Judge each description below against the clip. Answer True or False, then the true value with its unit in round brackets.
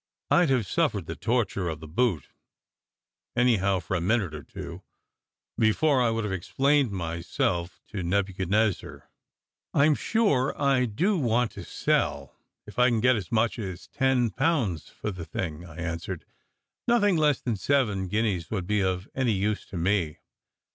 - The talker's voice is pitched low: True (105 Hz)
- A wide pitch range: True (5.7 semitones)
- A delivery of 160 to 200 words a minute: True (165 wpm)